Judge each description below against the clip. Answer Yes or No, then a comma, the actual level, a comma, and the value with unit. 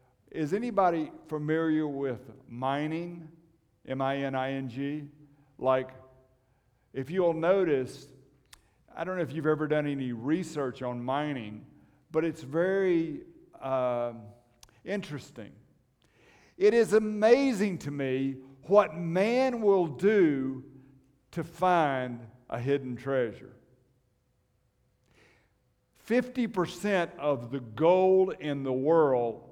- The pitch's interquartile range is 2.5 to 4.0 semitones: No, average, 4.8 semitones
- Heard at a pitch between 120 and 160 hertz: Yes, medium, 140 Hz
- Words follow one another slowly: Yes, slow, 105 wpm